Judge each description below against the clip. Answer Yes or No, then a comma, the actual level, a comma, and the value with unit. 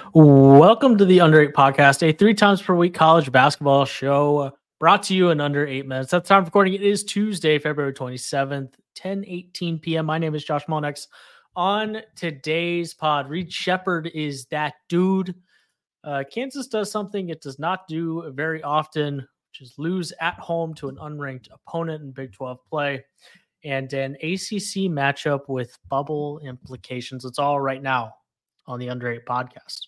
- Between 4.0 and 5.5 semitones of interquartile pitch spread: Yes, average, 4.5 semitones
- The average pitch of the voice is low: No, medium, 155 Hz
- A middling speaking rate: Yes, average, 175 wpm